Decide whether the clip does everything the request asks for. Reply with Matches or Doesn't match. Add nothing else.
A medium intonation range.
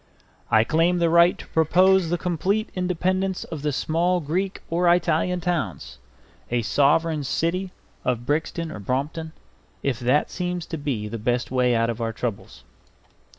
Doesn't match